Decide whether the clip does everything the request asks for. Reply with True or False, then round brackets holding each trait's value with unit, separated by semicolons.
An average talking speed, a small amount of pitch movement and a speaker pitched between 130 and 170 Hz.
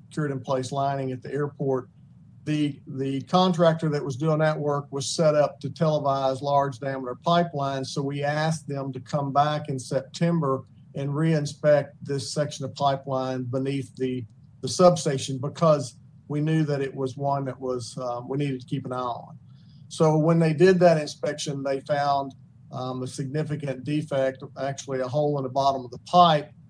True (180 wpm; 2.1 semitones; 140 Hz)